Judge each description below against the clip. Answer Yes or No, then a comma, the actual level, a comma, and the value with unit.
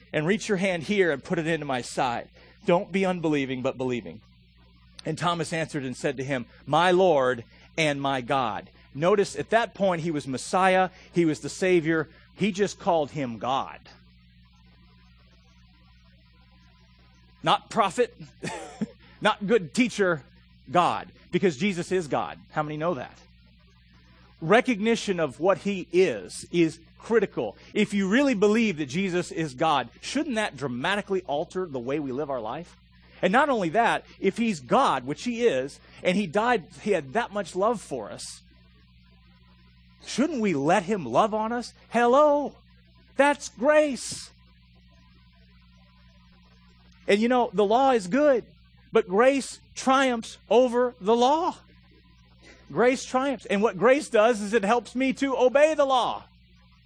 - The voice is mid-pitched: Yes, medium, 170 Hz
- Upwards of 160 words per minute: No, average, 150 wpm